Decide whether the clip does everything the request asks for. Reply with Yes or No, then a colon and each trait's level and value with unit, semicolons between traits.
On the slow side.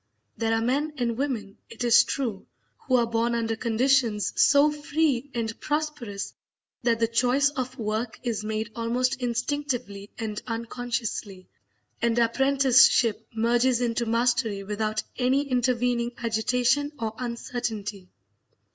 Yes: slow, 125 wpm